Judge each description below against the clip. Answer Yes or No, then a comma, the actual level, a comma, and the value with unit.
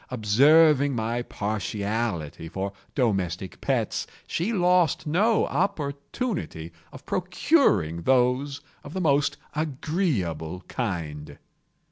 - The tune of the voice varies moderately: No, wide, 8.8 semitones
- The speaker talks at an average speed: No, slow, 90 wpm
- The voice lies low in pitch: Yes, low, 125 Hz